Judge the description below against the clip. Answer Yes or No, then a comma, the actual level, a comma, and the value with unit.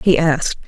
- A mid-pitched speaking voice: Yes, medium, 160 Hz